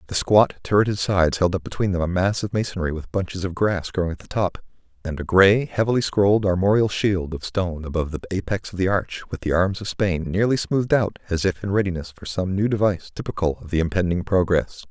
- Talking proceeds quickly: Yes, fast, 225 wpm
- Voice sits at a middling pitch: No, very low, 95 Hz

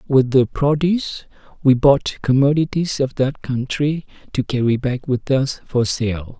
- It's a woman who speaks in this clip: No, male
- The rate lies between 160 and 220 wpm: No, average, 150 wpm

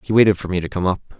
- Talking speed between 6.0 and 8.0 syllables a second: Yes, 7.3 syllables/s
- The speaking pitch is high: No, very low, 95 Hz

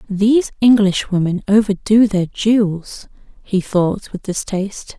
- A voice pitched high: Yes, high, 205 Hz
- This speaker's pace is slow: Yes, slow, 110 wpm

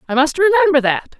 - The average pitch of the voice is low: No, very high, 300 Hz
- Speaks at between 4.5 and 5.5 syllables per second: No, 6.0 syllables/s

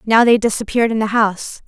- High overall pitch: Yes, high, 220 Hz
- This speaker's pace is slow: No, fast, 215 wpm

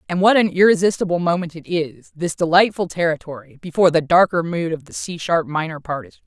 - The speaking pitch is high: No, medium, 170 Hz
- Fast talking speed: Yes, fast, 210 wpm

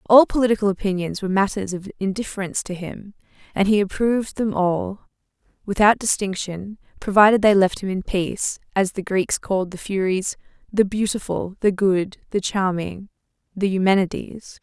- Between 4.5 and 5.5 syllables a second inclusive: Yes, 5.2 syllables/s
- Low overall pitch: No, high, 195 Hz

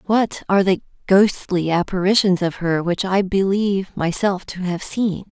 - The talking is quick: No, average, 155 wpm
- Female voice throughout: Yes, female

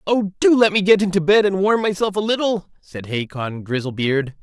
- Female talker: No, male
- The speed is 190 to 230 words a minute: Yes, fast, 205 wpm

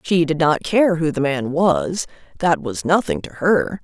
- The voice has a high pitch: No, medium, 165 Hz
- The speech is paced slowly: No, fast, 205 wpm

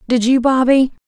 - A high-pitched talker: Yes, very high, 255 Hz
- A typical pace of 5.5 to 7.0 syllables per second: No, 5.0 syllables/s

